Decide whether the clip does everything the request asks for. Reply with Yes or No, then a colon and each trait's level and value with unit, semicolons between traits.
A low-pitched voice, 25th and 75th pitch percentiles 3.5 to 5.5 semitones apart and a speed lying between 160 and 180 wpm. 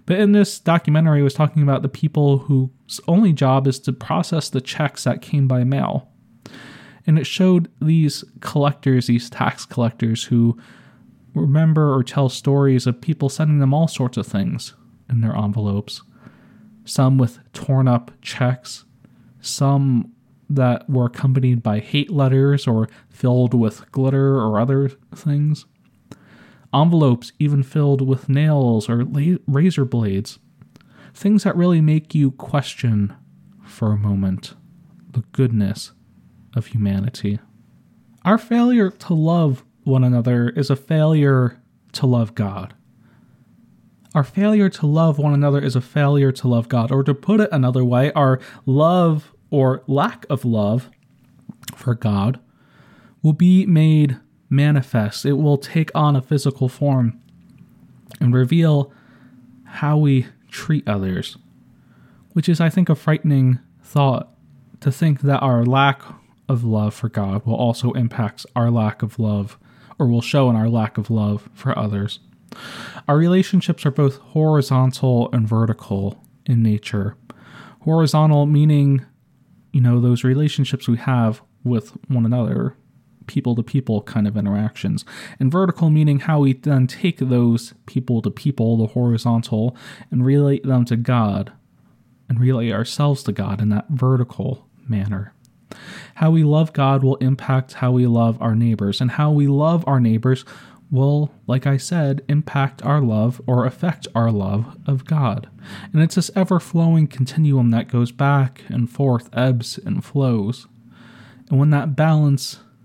No: low, 130 Hz; average, 3.8 semitones; average, 145 wpm